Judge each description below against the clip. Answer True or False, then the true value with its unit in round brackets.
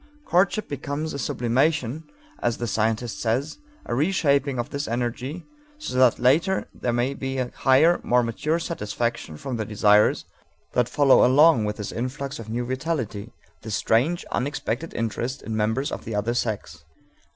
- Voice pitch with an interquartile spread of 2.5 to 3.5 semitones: False (3.9 semitones)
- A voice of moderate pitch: False (125 Hz)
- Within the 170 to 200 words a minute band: False (160 wpm)